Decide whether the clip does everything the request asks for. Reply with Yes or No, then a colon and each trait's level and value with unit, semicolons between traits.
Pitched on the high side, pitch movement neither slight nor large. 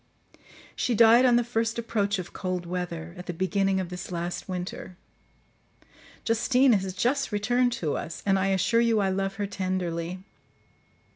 Yes: high, 195 Hz; average, 4.2 semitones